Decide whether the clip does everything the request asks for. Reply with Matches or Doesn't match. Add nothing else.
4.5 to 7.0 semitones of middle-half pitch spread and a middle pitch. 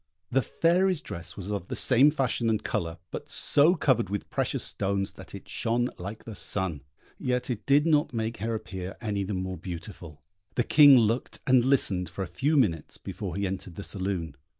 Doesn't match